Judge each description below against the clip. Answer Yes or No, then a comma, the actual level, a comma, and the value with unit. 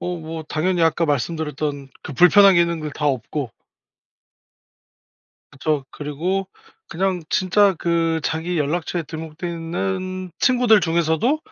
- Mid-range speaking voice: Yes, medium, 165 Hz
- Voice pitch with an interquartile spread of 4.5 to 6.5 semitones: No, average, 3.1 semitones